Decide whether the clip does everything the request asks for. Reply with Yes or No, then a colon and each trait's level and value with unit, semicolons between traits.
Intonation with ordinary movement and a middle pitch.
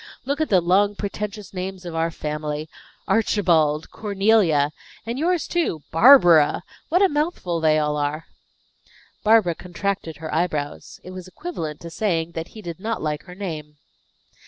Yes: average, 5.0 semitones; medium, 180 Hz